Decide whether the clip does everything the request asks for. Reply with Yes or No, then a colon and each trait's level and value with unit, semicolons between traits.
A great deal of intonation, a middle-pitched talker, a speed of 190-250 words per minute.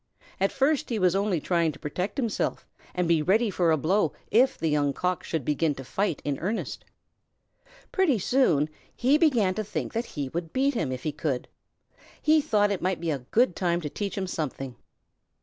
Yes: wide, 6.3 semitones; medium, 180 Hz; average, 200 wpm